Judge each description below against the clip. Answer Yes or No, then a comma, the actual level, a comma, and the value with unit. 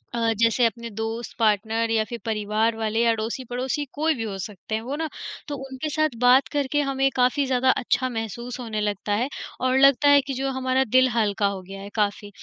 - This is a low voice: No, high, 235 Hz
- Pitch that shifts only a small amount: No, average, 3.4 semitones